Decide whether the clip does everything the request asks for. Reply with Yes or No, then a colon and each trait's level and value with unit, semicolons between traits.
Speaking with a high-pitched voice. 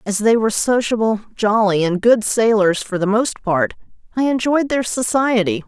Yes: high, 220 Hz